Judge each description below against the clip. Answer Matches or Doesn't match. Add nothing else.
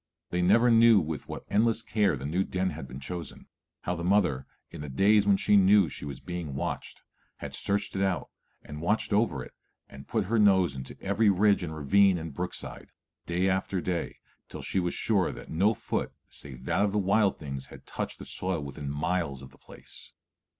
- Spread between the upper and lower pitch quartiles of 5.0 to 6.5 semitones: Matches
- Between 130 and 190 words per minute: Doesn't match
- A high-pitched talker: Doesn't match